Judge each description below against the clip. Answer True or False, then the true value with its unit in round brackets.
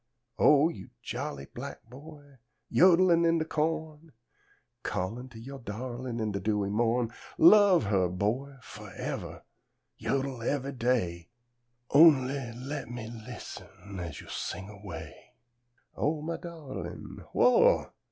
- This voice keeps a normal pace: False (125 wpm)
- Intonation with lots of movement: True (6.0 semitones)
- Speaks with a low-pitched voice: True (130 Hz)